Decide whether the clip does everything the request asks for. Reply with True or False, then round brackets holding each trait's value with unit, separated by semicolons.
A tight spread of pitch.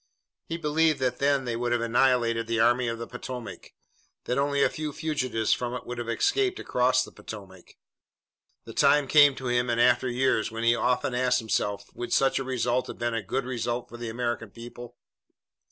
True (2.1 semitones)